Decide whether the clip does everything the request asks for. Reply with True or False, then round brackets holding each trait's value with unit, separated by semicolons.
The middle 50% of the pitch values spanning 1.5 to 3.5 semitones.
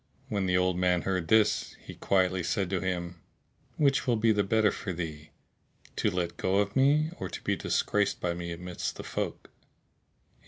True (2.8 semitones)